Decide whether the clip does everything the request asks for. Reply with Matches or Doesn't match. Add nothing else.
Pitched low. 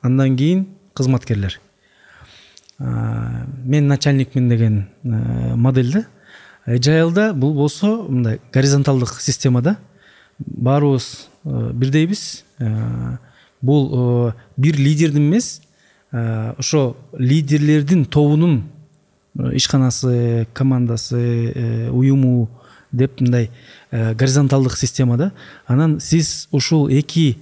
Matches